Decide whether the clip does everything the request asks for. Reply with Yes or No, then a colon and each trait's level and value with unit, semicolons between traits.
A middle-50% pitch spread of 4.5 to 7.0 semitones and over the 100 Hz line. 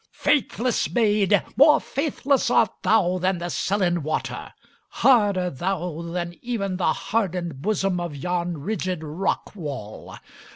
No: average, 3.9 semitones; medium, 185 Hz